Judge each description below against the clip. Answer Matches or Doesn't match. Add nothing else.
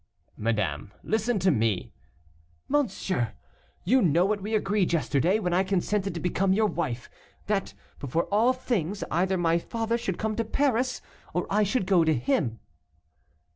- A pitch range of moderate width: Doesn't match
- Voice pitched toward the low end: Doesn't match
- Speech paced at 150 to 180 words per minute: Matches